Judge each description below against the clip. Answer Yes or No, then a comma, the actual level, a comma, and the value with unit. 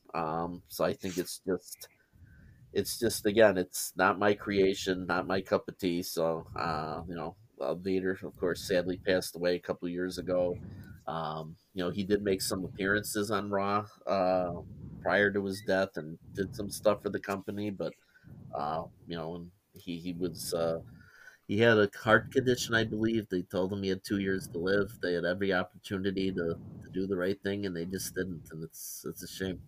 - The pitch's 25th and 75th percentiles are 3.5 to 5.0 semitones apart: No, narrow, 2.4 semitones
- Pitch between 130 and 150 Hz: No, very low, 95 Hz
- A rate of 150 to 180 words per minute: No, average, 200 wpm